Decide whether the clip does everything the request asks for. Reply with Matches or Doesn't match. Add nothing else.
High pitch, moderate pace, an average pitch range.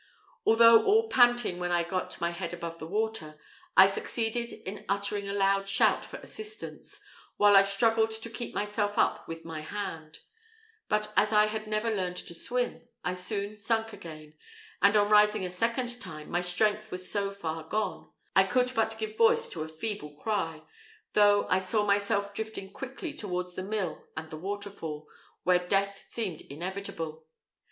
Matches